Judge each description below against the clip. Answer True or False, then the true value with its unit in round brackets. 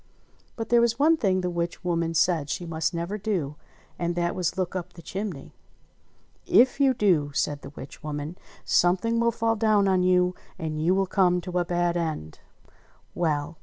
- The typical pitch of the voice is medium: True (180 Hz)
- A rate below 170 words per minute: False (185 wpm)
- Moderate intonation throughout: True (3.5 semitones)